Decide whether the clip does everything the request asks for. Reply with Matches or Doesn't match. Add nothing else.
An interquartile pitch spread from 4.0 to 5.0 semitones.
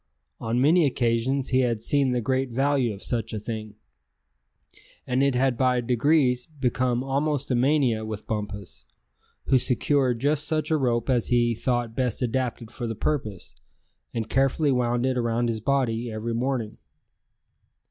Doesn't match